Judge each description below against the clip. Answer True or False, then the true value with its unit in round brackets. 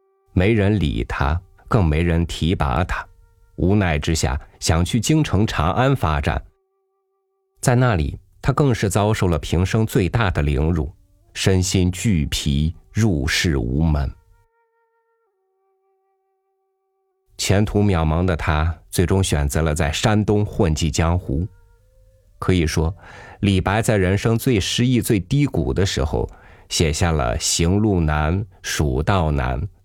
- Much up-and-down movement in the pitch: True (6.2 semitones)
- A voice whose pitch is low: True (95 Hz)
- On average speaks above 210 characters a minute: False (180 characters per minute)